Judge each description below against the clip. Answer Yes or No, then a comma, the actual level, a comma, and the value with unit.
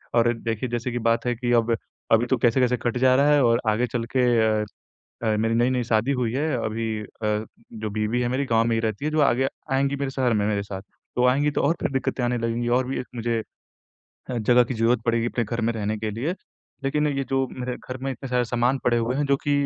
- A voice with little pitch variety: Yes, narrow, 2.3 semitones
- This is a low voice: Yes, low, 120 Hz